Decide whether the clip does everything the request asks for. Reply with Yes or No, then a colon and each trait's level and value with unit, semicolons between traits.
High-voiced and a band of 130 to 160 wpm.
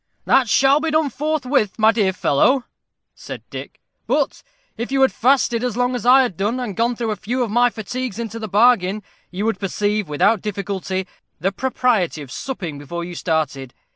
No: high, 220 Hz; average, 190 wpm